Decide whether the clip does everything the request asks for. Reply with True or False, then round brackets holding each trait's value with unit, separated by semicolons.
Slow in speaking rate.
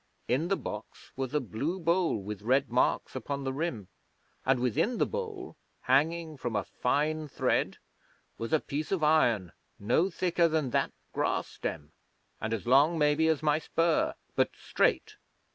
False (160 wpm)